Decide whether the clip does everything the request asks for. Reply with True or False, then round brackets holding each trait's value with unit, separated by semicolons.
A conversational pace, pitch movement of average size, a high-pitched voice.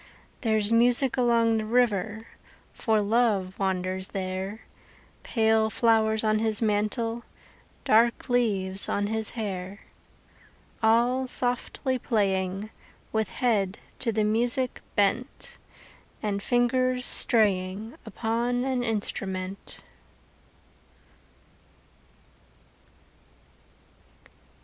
False (85 wpm; 3.0 semitones; 220 Hz)